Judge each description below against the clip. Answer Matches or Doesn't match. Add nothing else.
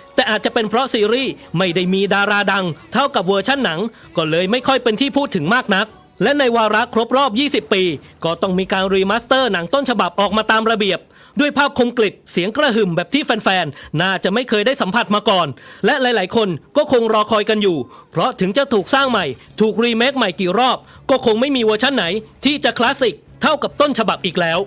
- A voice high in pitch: Matches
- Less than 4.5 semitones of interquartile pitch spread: Doesn't match